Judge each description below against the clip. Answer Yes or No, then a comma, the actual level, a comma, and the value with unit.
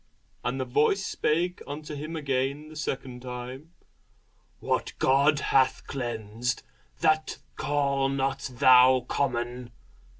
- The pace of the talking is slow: Yes, slow, 110 wpm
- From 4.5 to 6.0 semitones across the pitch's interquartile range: No, average, 3.0 semitones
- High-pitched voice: No, low, 135 Hz